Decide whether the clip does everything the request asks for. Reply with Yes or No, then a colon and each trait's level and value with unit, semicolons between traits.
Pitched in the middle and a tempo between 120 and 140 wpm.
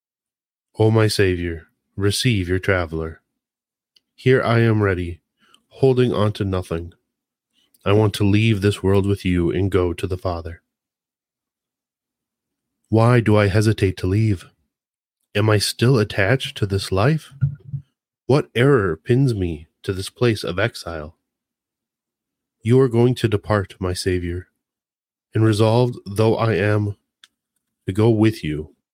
No: low, 105 Hz; slow, 135 wpm